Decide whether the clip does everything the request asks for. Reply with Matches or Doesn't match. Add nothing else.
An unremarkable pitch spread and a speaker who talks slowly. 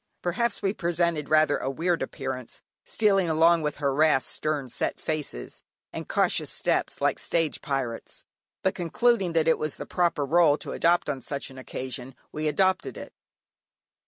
Doesn't match